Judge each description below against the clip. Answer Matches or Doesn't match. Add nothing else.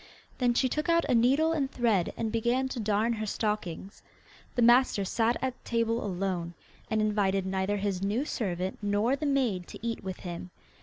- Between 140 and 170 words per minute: Doesn't match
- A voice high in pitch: Matches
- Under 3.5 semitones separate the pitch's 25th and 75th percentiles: Doesn't match